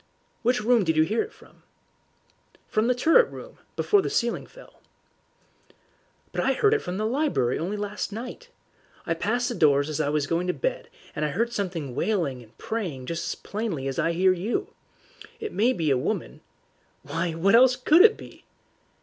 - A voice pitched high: Yes, high, 205 Hz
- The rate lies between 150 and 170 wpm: No, average, 190 wpm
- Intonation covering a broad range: Yes, wide, 7.5 semitones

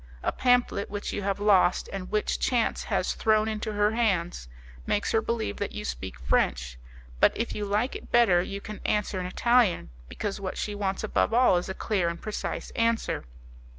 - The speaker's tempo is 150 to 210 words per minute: Yes, average, 190 wpm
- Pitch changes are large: No, average, 3.4 semitones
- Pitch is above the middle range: Yes, high, 205 Hz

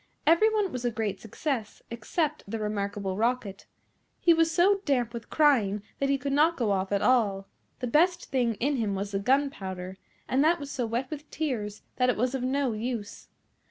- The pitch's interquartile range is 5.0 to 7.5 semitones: Yes, wide, 5.5 semitones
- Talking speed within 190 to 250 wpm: Yes, average, 195 wpm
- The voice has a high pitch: Yes, very high, 250 Hz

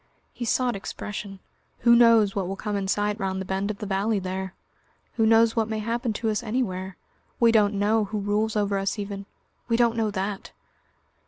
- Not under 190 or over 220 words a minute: Yes, average, 195 wpm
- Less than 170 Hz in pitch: No, high, 210 Hz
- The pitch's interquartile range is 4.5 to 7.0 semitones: No, narrow, 2.4 semitones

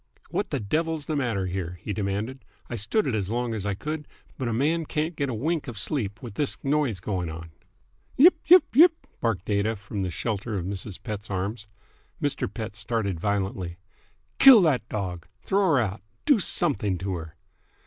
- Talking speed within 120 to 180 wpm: No, average, 190 wpm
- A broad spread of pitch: Yes, wide, 6.9 semitones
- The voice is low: Yes, low, 110 Hz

